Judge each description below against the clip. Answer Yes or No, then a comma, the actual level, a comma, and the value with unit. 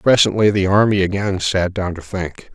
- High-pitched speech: No, very low, 95 Hz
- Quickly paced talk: No, average, 190 wpm